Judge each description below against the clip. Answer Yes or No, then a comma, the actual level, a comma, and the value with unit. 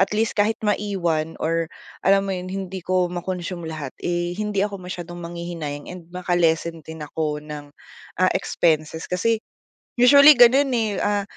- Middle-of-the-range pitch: Yes, medium, 180 Hz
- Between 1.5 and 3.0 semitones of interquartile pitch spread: No, average, 3.5 semitones